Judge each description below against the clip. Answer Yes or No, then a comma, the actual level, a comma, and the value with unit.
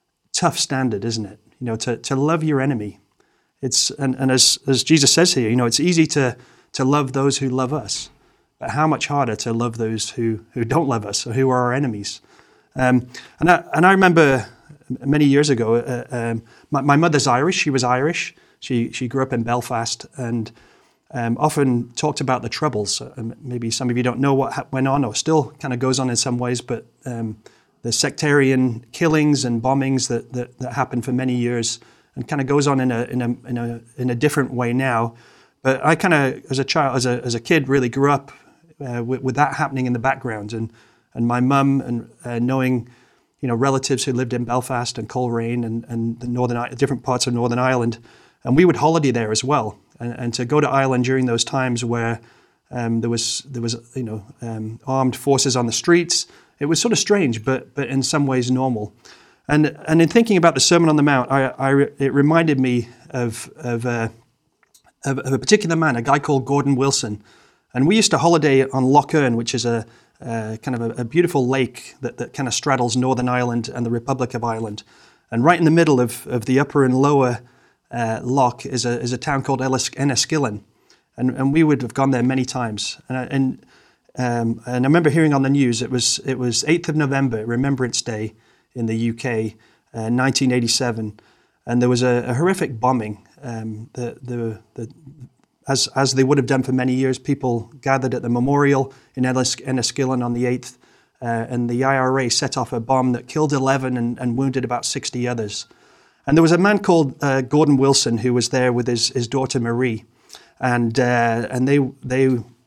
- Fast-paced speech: Yes, fast, 210 wpm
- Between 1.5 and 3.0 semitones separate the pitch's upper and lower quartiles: Yes, narrow, 2.6 semitones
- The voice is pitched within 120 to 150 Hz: Yes, low, 130 Hz